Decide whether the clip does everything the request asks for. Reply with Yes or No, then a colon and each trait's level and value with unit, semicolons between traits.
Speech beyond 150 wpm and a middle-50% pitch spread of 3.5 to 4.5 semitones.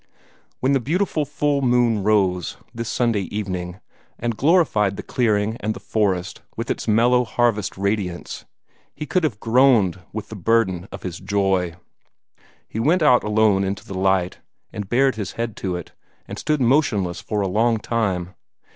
Yes: average, 165 wpm; average, 4.1 semitones